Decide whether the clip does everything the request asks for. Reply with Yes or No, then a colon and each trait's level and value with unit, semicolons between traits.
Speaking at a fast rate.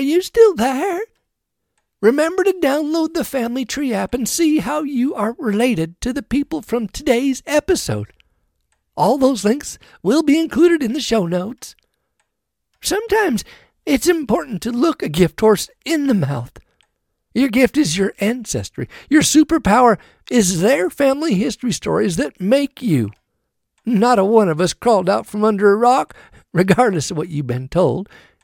No: average, 160 wpm